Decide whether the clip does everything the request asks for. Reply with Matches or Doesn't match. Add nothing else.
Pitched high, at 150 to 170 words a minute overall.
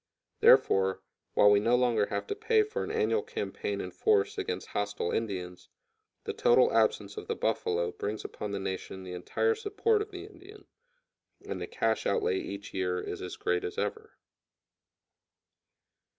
Matches